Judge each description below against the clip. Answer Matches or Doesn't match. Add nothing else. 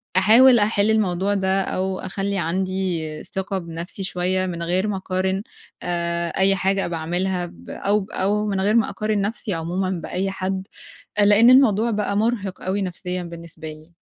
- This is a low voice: Doesn't match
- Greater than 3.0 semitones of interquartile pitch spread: Doesn't match